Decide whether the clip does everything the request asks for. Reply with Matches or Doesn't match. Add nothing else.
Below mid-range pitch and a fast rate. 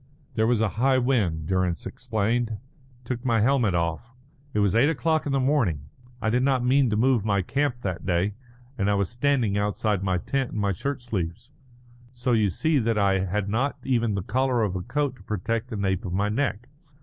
Matches